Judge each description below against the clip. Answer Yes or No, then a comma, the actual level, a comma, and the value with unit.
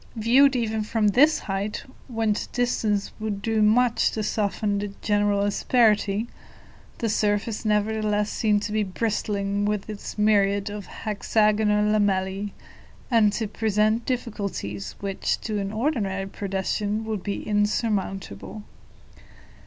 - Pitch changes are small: Yes, narrow, 1.5 semitones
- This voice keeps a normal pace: No, slow, 120 wpm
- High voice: Yes, high, 210 Hz